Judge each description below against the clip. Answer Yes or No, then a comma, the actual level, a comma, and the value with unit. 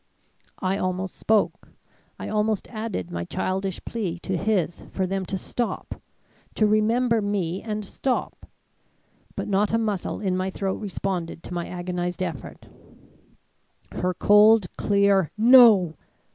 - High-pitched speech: Yes, high, 195 Hz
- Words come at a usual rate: No, slow, 130 wpm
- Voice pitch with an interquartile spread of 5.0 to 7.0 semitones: No, average, 2.8 semitones